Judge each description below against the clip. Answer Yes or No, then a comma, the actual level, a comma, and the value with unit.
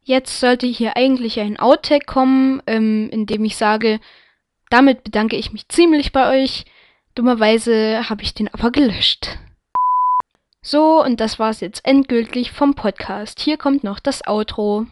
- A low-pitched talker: No, high, 235 Hz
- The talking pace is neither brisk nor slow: Yes, average, 155 wpm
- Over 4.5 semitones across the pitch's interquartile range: No, average, 3.9 semitones